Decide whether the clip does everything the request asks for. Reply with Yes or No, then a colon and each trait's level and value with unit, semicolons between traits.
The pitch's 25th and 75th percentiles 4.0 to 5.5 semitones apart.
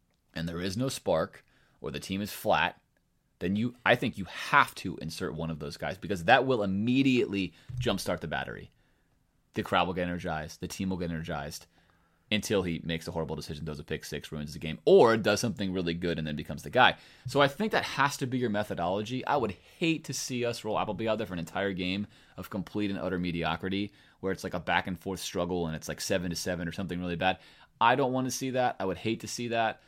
Yes: average, 4.8 semitones